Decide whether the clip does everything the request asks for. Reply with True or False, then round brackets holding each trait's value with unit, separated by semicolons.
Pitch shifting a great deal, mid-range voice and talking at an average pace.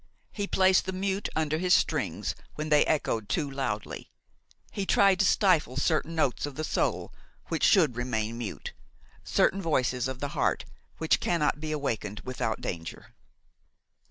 True (6.3 semitones; 150 Hz; 155 wpm)